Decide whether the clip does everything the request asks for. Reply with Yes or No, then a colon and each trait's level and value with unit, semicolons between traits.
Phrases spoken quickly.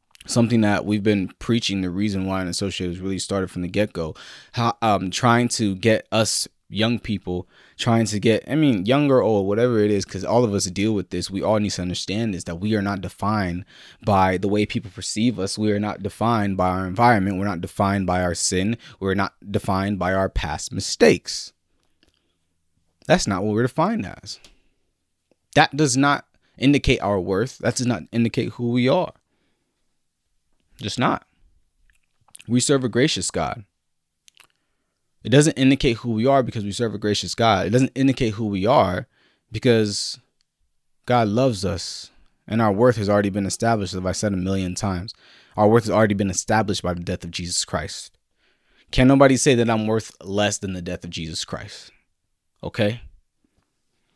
No: average, 185 wpm